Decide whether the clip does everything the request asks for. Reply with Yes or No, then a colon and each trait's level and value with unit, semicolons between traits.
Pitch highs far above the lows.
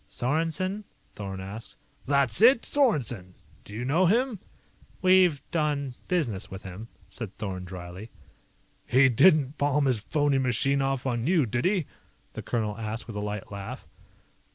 Yes: wide, 6.9 semitones